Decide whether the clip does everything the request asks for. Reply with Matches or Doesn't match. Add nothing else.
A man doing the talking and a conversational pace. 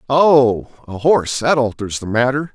Matches